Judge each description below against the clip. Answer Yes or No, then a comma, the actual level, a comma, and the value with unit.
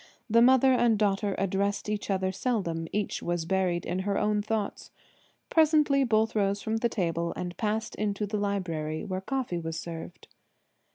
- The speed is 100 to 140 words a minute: No, average, 165 wpm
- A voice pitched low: No, high, 200 Hz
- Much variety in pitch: No, average, 3.7 semitones